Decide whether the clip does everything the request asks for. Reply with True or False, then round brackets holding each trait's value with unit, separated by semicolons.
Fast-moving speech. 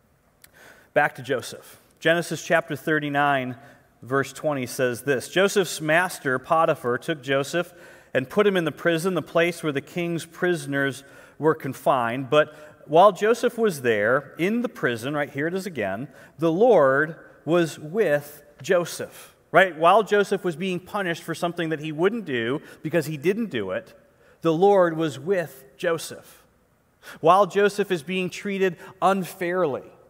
False (150 wpm)